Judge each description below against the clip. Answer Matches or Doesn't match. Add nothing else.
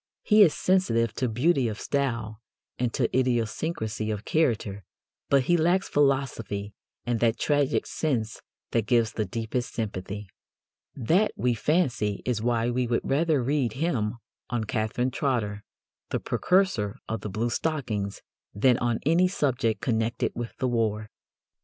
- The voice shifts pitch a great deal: Doesn't match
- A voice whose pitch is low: Matches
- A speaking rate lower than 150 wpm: Matches